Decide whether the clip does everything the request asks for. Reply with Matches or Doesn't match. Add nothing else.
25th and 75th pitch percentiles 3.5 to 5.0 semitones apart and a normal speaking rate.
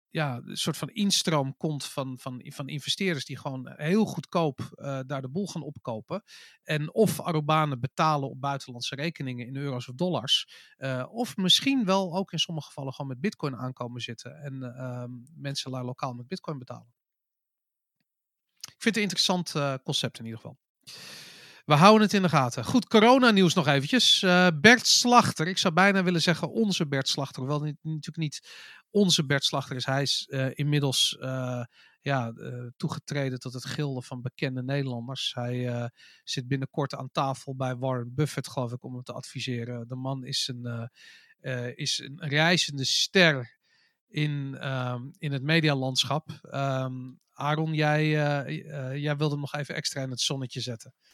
Matches